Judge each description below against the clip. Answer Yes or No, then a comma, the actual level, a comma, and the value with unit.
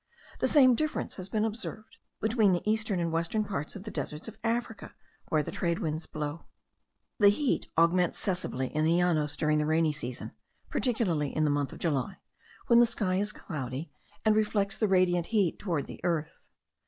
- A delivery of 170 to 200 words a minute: Yes, average, 185 wpm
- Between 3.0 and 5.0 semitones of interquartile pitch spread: No, wide, 5.6 semitones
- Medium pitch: Yes, medium, 180 Hz